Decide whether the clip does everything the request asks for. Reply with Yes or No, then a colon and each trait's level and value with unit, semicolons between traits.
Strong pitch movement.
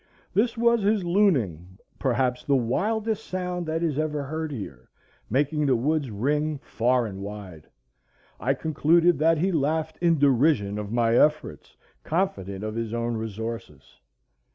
Yes: wide, 6.4 semitones